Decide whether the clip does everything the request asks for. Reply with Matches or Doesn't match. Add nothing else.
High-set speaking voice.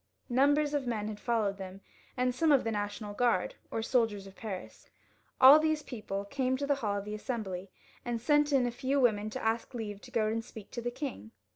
Matches